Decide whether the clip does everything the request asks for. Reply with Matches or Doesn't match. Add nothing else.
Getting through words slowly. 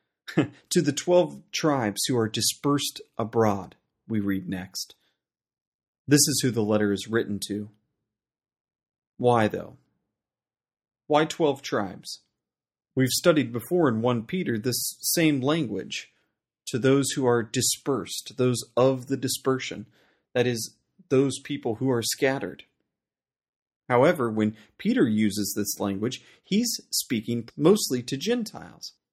Matches